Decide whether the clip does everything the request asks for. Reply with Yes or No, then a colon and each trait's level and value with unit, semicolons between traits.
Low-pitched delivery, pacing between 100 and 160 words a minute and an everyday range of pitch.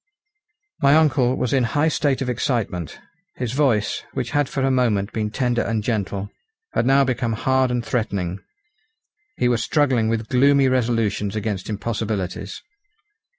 Yes: low, 120 Hz; average, 150 wpm; average, 3.6 semitones